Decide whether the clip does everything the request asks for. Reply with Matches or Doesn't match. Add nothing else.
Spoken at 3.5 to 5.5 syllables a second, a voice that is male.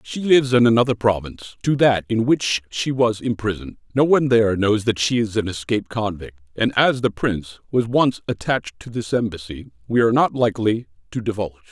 Doesn't match